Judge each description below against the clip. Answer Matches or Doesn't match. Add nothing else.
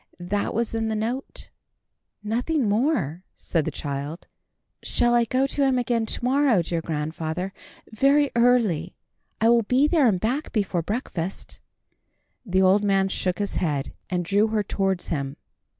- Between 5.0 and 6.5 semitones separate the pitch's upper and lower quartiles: Matches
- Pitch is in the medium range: Doesn't match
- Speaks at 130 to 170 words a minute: Matches